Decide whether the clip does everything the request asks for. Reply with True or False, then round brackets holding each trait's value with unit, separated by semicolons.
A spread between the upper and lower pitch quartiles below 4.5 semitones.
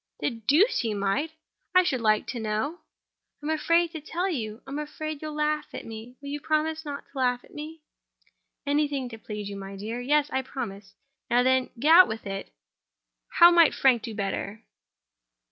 False (5.6 semitones)